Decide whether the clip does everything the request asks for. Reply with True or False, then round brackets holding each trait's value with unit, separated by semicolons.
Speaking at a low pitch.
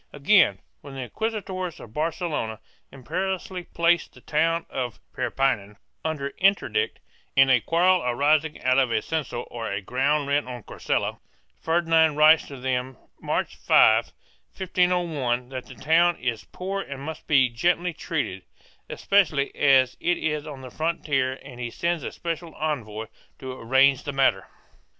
False (145 Hz)